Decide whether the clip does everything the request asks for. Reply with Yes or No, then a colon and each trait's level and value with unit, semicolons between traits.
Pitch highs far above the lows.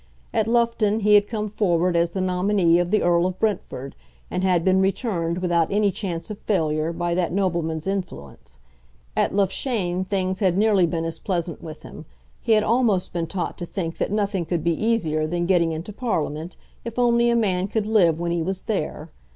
No: average, 3.7 semitones